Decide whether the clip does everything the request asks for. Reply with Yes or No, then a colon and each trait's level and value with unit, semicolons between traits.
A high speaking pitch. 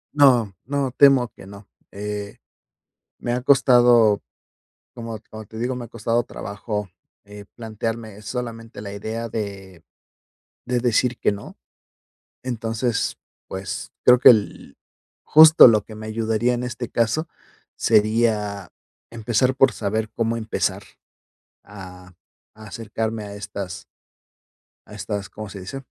No: low, 110 Hz